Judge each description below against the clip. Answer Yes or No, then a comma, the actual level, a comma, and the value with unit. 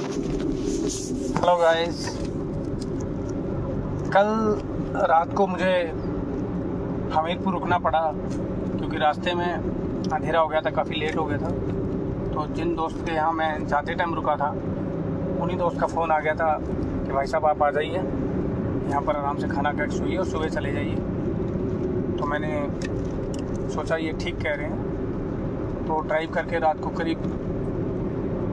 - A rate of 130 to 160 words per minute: Yes, average, 145 wpm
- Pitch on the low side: No, medium, 160 Hz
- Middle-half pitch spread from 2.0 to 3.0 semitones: Yes, narrow, 2.4 semitones